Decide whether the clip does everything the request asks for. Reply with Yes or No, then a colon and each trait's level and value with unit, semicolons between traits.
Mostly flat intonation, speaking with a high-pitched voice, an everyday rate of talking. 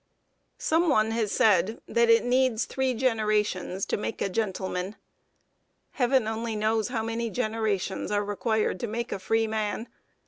Yes: narrow, 2.1 semitones; high, 220 Hz; average, 150 wpm